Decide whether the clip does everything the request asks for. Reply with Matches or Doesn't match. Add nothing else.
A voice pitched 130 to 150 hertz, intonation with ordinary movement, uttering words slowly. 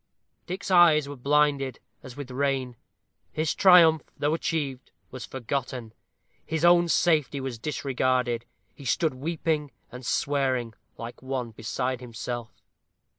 Matches